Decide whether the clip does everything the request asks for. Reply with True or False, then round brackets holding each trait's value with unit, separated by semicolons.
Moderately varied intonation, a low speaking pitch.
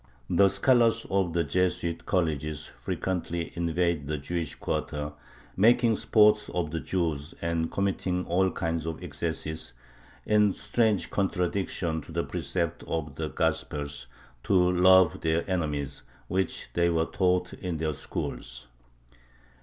True (3.0 semitones; 85 Hz)